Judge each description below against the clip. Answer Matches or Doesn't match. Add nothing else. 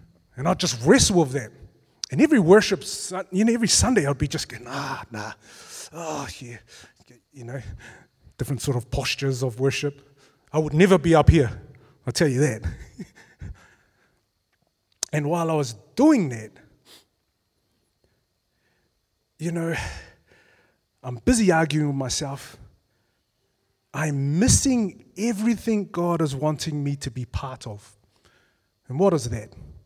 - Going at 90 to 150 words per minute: Matches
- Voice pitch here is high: Doesn't match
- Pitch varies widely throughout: Matches